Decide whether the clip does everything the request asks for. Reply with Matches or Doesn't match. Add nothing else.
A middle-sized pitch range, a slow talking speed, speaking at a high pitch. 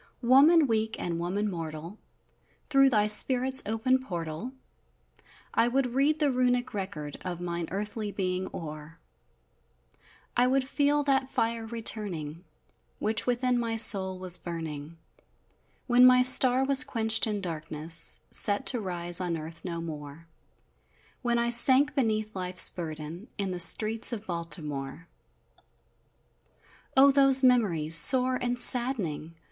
Doesn't match